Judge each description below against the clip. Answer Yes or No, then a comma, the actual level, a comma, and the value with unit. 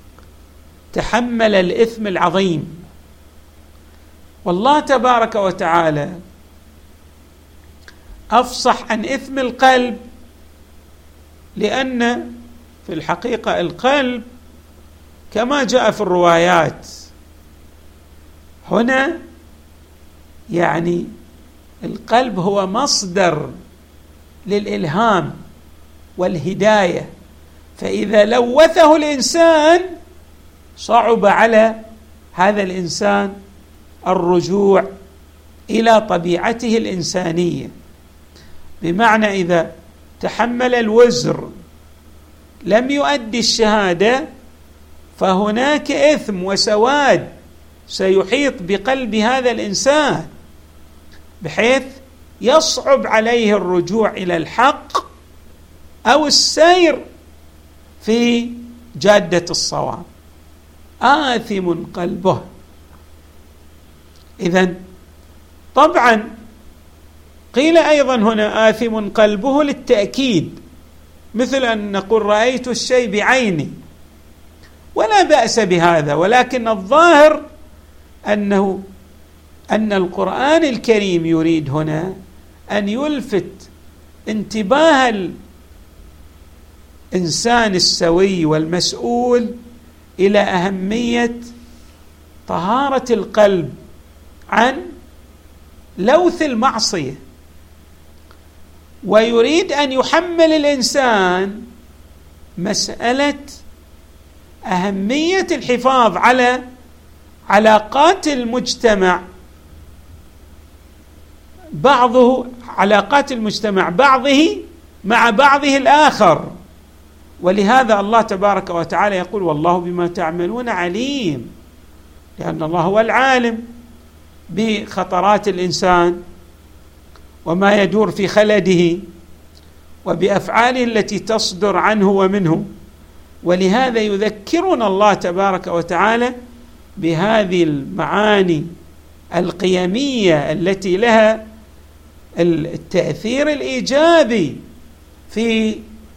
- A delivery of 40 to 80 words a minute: Yes, slow, 65 wpm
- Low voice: No, medium, 185 Hz